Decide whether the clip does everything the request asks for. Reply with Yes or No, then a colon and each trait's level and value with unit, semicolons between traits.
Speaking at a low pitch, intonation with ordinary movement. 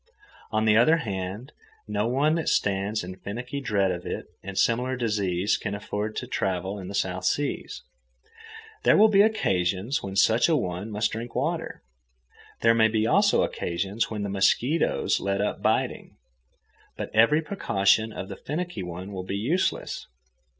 Yes: low, 105 Hz; average, 4.4 semitones